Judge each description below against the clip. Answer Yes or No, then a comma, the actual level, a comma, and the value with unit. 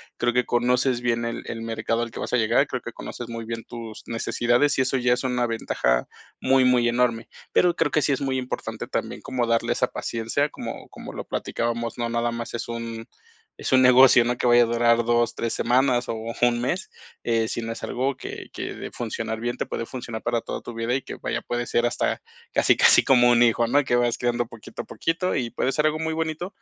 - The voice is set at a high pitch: No, low, 120 Hz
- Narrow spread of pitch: Yes, narrow, 1.5 semitones